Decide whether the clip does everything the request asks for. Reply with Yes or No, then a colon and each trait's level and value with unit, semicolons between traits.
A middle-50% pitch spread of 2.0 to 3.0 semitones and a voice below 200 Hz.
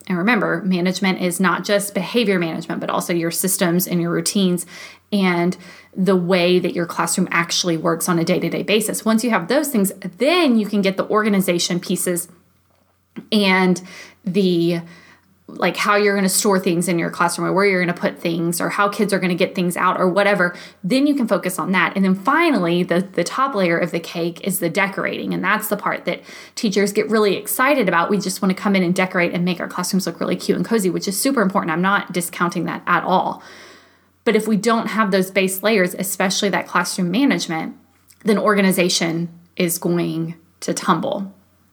Yes: narrow, 2.6 semitones; medium, 185 Hz